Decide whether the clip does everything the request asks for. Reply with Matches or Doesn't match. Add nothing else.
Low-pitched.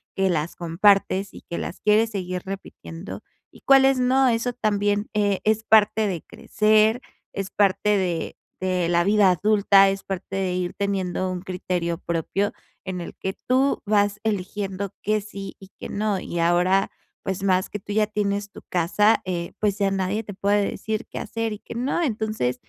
Doesn't match